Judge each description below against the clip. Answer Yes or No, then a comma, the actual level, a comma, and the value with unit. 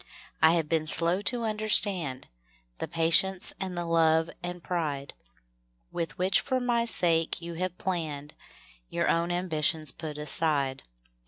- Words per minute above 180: No, slow, 135 wpm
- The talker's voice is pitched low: No, medium, 165 Hz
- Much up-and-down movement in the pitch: No, average, 2.8 semitones